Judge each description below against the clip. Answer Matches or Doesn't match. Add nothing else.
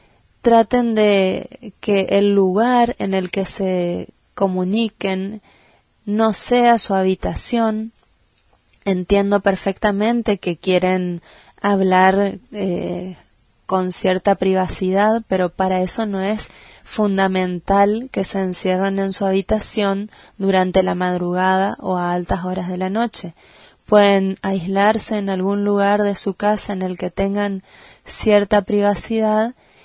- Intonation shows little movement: Matches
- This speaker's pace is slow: Matches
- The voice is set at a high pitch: Matches